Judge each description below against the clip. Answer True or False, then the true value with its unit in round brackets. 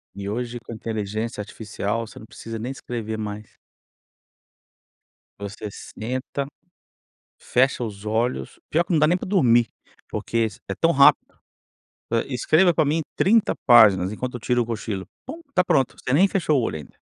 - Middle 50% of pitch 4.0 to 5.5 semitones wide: True (4.7 semitones)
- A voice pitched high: False (120 Hz)